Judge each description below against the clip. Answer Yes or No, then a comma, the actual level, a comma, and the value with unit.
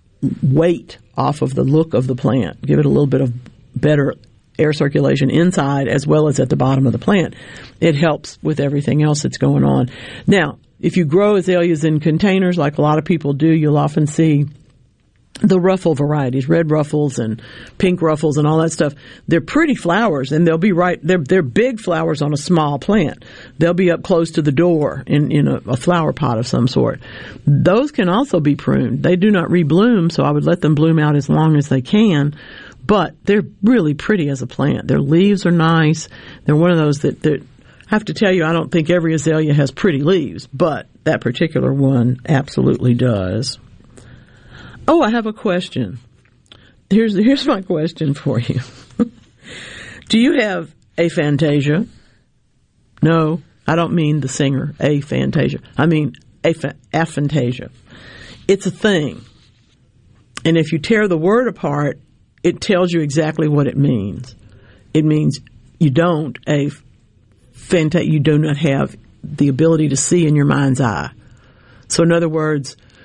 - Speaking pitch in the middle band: Yes, medium, 150 Hz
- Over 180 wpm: No, average, 175 wpm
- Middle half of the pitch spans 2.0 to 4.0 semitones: No, average, 4.6 semitones